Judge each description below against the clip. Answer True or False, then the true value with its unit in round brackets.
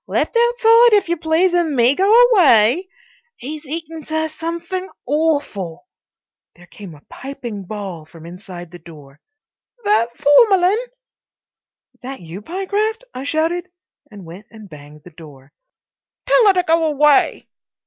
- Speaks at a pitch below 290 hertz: False (295 Hz)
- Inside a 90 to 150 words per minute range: True (140 wpm)